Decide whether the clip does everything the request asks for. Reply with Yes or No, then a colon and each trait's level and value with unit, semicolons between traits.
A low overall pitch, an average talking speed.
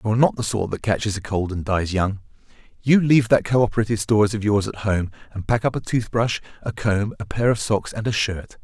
No: low, 105 Hz; fast, 245 wpm